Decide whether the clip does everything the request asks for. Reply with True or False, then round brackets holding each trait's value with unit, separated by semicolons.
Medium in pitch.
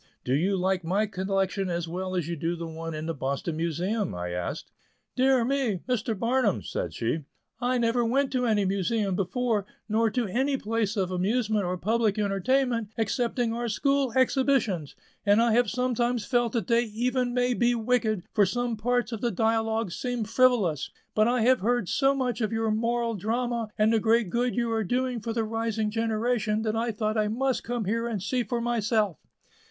False (225 Hz)